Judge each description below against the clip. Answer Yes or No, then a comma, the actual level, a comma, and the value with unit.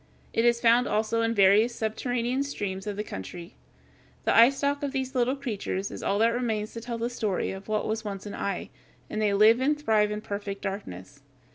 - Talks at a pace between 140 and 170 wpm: No, fast, 205 wpm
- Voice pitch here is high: Yes, high, 220 Hz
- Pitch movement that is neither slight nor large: Yes, average, 3.1 semitones